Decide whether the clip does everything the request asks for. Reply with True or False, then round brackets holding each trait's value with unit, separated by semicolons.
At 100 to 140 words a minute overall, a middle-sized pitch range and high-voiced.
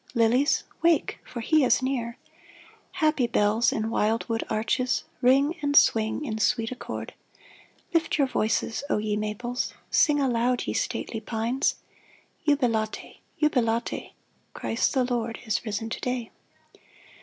True (135 wpm; 3.0 semitones; 240 Hz)